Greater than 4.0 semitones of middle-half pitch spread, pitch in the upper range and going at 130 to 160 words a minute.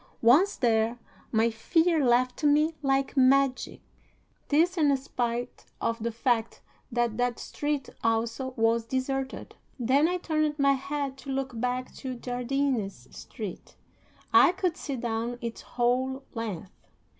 No: average, 3.0 semitones; very high, 255 Hz; slow, 135 wpm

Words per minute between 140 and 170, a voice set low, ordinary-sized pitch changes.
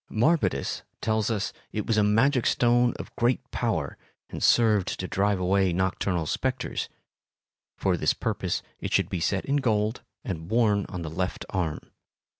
Yes: average, 160 wpm; low, 105 Hz; average, 4.3 semitones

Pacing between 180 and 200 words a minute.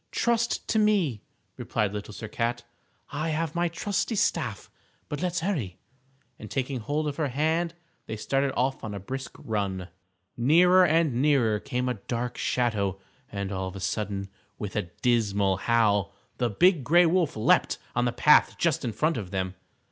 No: average, 170 wpm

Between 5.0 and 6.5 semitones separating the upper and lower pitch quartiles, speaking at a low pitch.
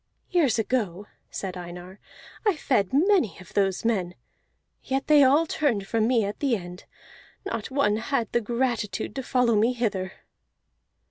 No: average, 5.3 semitones; high, 230 Hz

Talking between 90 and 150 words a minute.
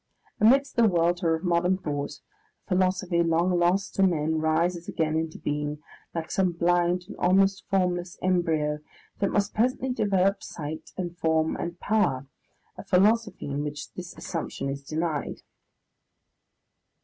Yes: average, 140 wpm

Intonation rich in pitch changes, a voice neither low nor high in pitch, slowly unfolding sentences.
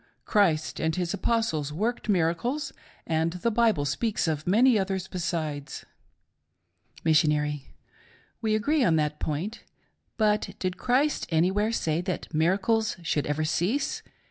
Yes: wide, 5.7 semitones; medium, 180 Hz; slow, 125 wpm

